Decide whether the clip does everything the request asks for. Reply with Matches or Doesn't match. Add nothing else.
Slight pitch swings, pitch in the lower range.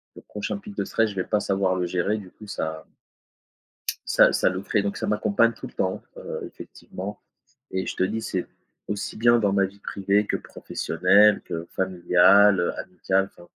Matches